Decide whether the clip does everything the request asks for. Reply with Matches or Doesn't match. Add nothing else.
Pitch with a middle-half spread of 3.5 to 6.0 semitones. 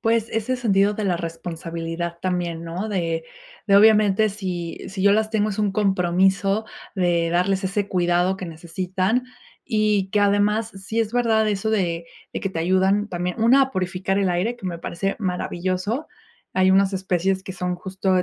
Doesn't match